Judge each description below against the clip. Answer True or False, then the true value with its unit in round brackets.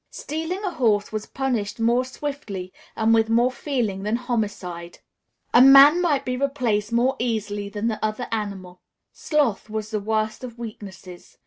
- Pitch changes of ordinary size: True (3.7 semitones)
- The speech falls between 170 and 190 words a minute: False (155 wpm)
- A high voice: True (225 Hz)